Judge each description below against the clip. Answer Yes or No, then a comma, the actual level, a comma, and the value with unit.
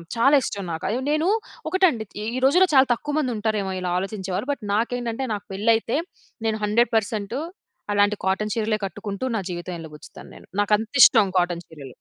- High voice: Yes, high, 215 Hz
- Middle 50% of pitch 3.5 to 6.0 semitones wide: Yes, average, 3.8 semitones